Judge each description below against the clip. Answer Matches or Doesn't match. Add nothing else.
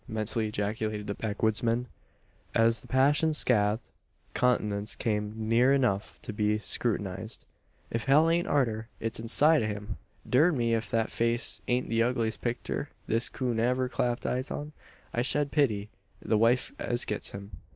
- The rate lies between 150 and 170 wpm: Matches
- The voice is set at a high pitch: Doesn't match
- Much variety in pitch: Doesn't match